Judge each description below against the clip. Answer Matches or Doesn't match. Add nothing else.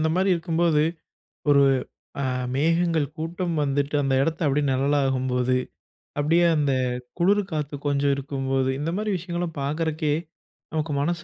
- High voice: Doesn't match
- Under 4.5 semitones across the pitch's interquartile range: Matches